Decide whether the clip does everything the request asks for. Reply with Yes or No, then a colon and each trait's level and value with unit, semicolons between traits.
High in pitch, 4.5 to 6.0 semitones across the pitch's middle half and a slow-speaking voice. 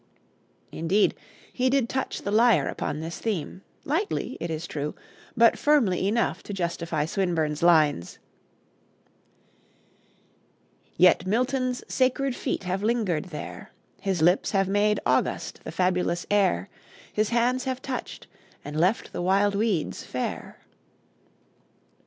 Yes: high, 195 Hz; wide, 5.6 semitones; slow, 120 wpm